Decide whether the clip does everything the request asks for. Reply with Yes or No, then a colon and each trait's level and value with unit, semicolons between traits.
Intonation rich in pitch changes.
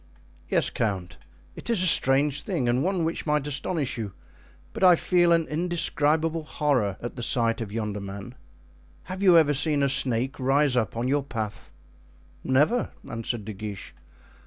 Yes: wide, 5.7 semitones